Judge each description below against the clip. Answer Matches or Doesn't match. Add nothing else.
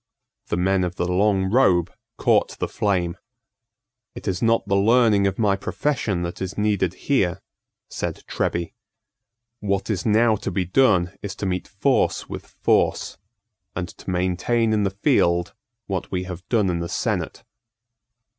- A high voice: Doesn't match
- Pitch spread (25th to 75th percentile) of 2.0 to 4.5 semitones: Matches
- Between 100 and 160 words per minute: Matches